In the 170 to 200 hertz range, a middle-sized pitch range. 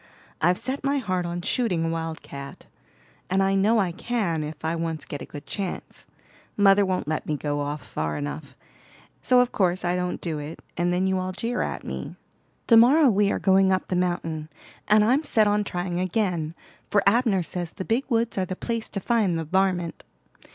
Yes: medium, 185 Hz; average, 4.2 semitones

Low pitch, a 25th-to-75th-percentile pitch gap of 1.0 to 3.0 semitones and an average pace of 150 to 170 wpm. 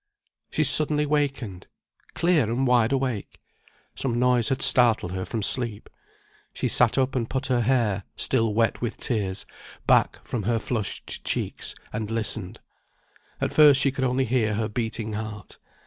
No: low, 120 Hz; average, 3.4 semitones; average, 155 wpm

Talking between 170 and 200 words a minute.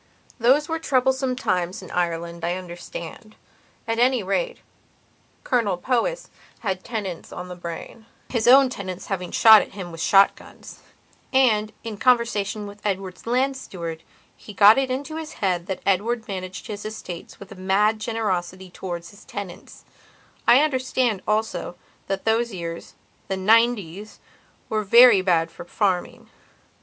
No: average, 140 wpm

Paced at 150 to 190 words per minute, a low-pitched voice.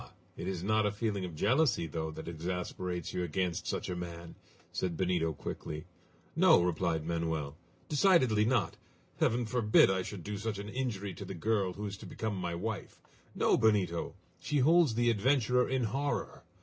Yes: average, 175 wpm; low, 100 Hz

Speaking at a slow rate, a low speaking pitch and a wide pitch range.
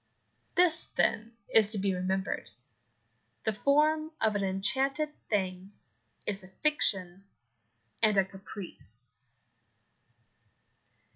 No: slow, 95 wpm; high, 205 Hz; wide, 5.7 semitones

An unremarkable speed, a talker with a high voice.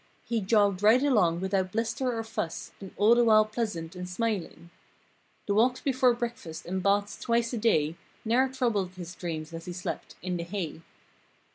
Yes: average, 170 wpm; high, 205 Hz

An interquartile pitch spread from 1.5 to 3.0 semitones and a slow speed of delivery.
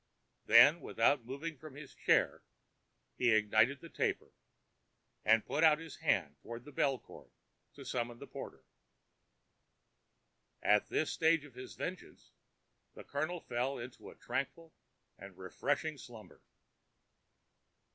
No: average, 4.7 semitones; slow, 125 wpm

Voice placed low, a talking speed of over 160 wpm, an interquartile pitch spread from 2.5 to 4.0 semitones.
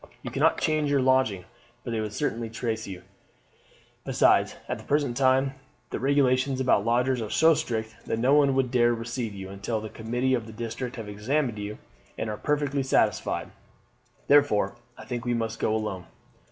Yes: low, 120 Hz; average, 180 wpm; average, 3.3 semitones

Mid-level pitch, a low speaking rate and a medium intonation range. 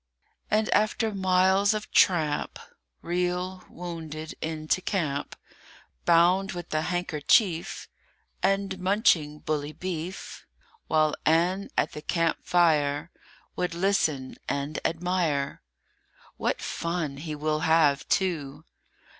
Yes: medium, 170 Hz; slow, 105 wpm; average, 3.2 semitones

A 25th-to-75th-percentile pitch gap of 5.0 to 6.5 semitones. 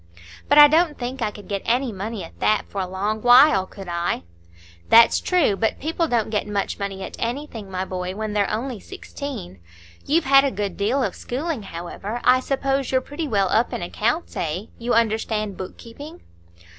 Yes: wide, 5.4 semitones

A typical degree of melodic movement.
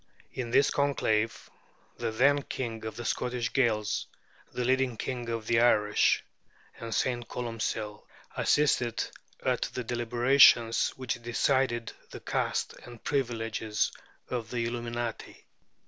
No: narrow, 1.8 semitones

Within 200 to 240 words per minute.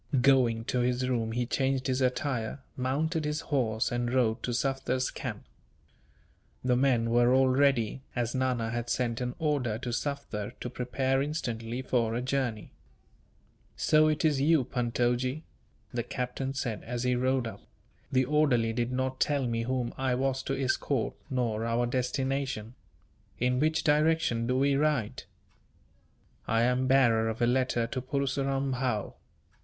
No: average, 155 wpm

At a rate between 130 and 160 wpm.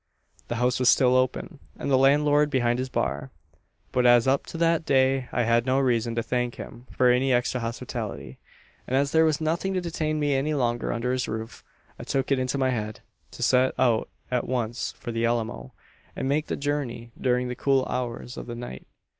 No: fast, 205 wpm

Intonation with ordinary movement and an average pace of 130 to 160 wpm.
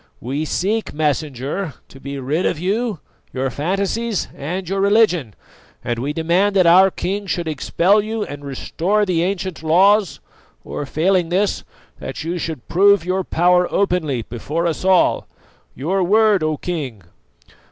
Yes: average, 4.7 semitones; average, 150 wpm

